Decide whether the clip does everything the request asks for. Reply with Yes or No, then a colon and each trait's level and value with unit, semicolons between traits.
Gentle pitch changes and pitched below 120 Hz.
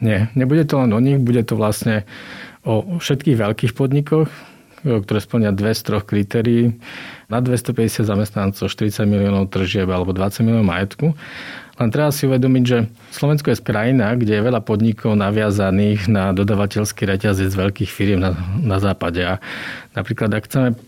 No: average, 3.5 semitones; low, 110 Hz